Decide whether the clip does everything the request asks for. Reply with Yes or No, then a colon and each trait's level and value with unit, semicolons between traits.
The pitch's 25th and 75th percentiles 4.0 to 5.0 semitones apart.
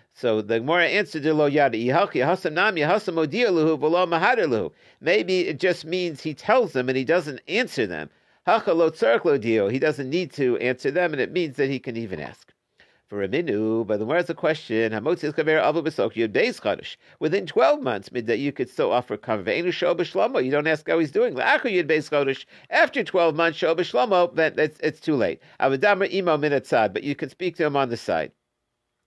Yes: average, 4.6 semitones